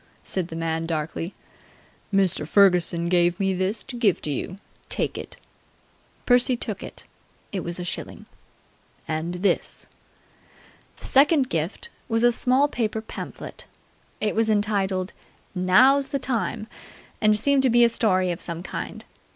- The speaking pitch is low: No, high, 200 Hz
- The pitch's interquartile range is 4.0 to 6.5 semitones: Yes, average, 5.3 semitones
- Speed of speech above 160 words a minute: No, average, 145 wpm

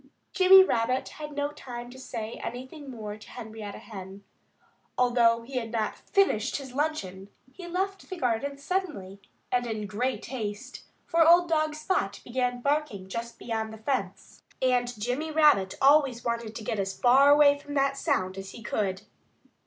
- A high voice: Yes, high, 245 Hz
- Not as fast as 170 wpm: Yes, average, 160 wpm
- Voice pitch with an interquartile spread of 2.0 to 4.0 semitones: No, average, 4.9 semitones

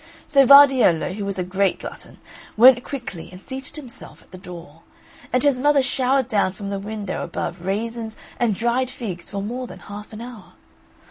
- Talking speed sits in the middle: Yes, average, 185 wpm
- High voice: Yes, high, 220 Hz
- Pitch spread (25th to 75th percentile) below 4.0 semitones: No, average, 4.8 semitones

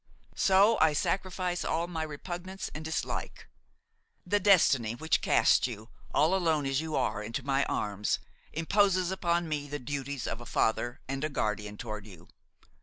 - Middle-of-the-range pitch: Yes, medium, 150 Hz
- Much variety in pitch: Yes, wide, 6.6 semitones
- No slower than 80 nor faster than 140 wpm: No, average, 160 wpm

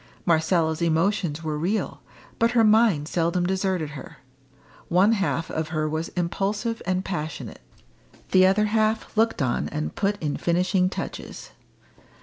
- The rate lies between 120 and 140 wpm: Yes, slow, 135 wpm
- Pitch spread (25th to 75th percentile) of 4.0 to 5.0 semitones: Yes, average, 4.3 semitones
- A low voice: No, medium, 180 Hz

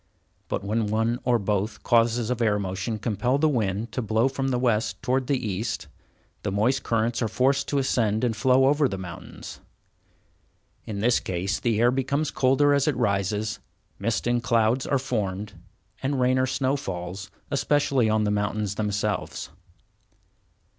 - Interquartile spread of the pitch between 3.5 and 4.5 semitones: Yes, average, 3.9 semitones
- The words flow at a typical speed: Yes, average, 165 wpm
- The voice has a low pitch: Yes, low, 115 Hz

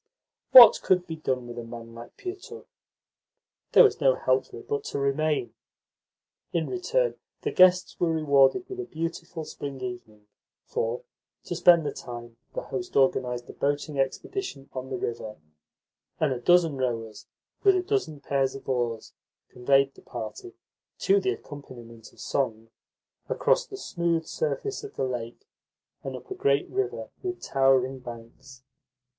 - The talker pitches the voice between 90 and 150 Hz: Yes, medium, 140 Hz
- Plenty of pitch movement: Yes, wide, 6.3 semitones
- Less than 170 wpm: Yes, average, 155 wpm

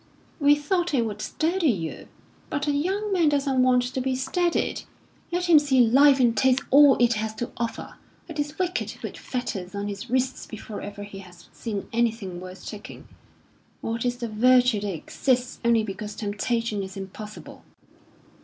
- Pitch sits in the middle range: No, high, 245 Hz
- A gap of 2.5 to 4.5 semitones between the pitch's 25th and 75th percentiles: No, average, 5.3 semitones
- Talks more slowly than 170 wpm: No, average, 175 wpm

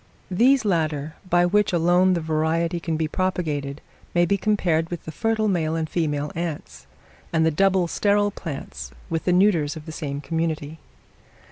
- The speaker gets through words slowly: No, average, 165 wpm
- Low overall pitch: No, medium, 165 Hz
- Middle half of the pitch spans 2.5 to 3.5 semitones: Yes, average, 2.9 semitones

